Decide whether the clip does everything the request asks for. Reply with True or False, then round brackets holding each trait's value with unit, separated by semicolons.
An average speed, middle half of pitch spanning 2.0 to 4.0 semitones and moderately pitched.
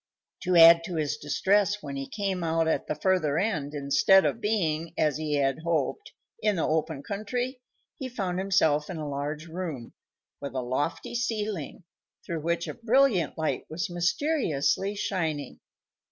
False (160 wpm; 4.8 semitones; 165 Hz)